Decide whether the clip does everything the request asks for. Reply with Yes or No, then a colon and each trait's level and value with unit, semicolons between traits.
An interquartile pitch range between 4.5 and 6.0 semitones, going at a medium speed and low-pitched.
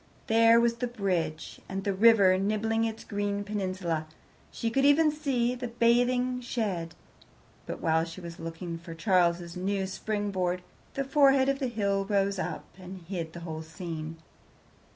No: average, 5.1 semitones; average, 155 wpm; high, 200 Hz